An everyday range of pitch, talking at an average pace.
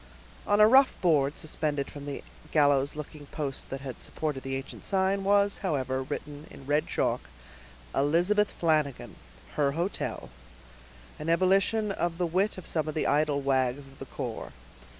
Yes: average, 4.9 semitones; average, 160 wpm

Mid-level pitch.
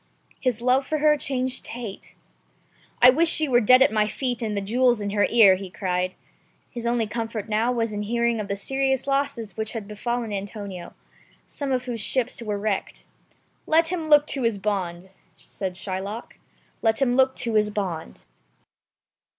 No: high, 230 Hz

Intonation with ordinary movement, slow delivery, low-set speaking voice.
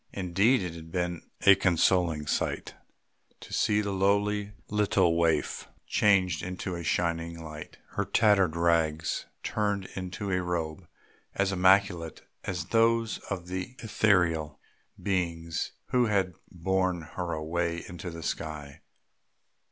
Yes: average, 3.1 semitones; slow, 125 wpm; very low, 90 Hz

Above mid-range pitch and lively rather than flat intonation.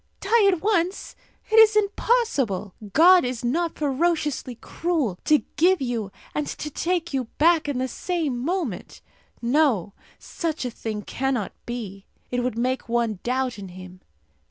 Yes: very high, 270 Hz; wide, 6.4 semitones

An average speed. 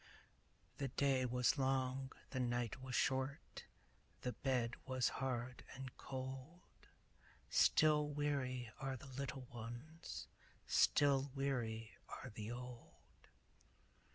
No: slow, 105 wpm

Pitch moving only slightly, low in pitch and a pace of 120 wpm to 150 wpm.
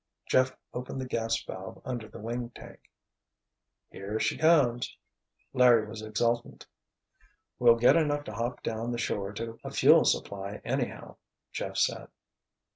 Yes: narrow, 2.3 semitones; low, 115 Hz; average, 140 wpm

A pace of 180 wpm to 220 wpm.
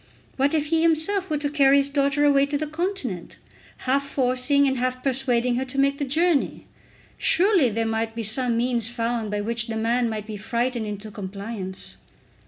Yes: average, 190 wpm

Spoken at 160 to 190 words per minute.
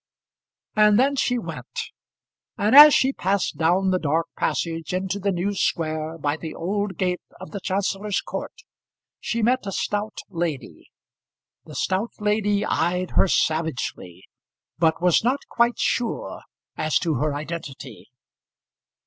No: average, 140 wpm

